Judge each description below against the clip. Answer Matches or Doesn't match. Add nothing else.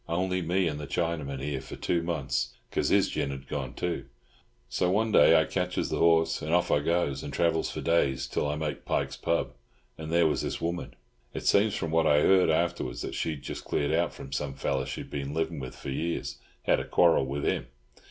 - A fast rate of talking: Matches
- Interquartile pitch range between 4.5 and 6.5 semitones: Doesn't match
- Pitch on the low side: Matches